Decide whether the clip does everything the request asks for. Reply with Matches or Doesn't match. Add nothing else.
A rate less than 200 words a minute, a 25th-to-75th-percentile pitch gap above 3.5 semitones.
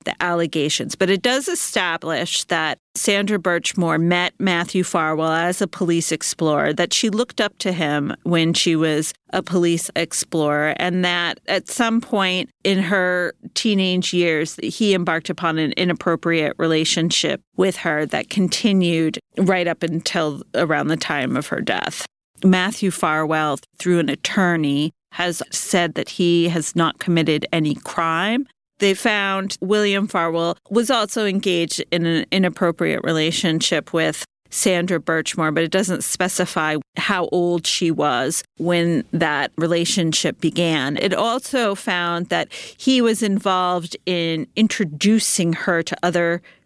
Doesn't match